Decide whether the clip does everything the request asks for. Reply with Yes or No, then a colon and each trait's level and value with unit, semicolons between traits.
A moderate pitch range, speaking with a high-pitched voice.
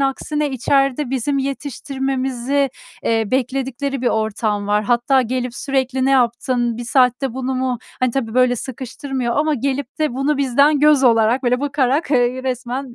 No: narrow, 2.2 semitones; very high, 260 Hz